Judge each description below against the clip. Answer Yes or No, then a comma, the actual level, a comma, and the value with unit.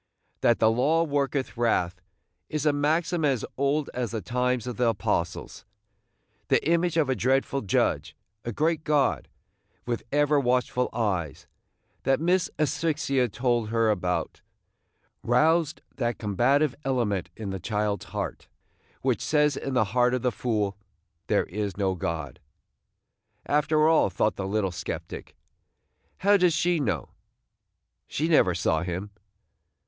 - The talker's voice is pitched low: Yes, low, 125 Hz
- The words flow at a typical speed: Yes, average, 145 wpm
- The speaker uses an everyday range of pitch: No, wide, 6.1 semitones